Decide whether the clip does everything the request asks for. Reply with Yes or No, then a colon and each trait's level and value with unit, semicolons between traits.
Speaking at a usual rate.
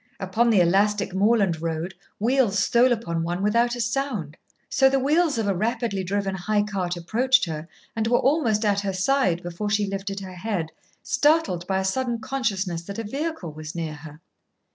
Yes: average, 180 wpm